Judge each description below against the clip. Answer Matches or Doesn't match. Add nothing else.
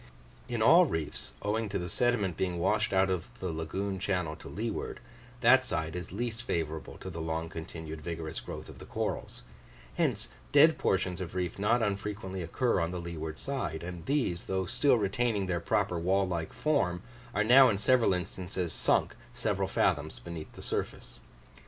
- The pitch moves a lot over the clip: Doesn't match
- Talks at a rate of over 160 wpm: Matches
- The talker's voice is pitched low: Matches